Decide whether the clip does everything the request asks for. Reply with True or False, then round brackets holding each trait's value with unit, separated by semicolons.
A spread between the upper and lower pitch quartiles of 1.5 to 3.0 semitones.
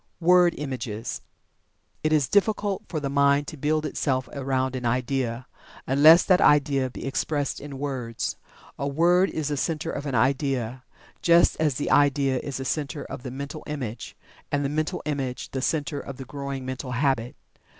True (2.5 semitones)